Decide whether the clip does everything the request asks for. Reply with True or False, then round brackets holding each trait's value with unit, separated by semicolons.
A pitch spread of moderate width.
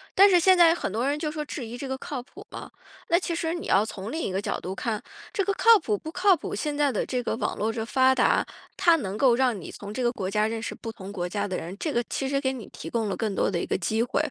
False (6.4 semitones)